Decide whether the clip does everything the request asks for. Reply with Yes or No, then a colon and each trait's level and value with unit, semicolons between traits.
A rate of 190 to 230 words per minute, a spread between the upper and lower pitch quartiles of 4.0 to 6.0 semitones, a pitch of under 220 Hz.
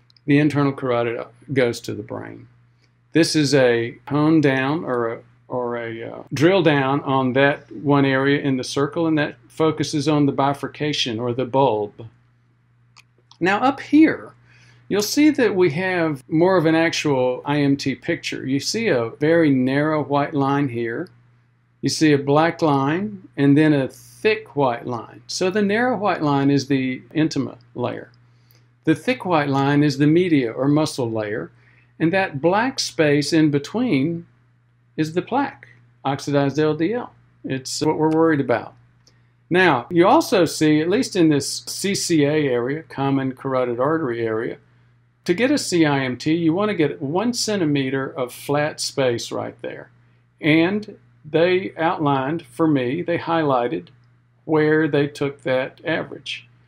No: average, 150 wpm; average, 4.6 semitones; medium, 140 Hz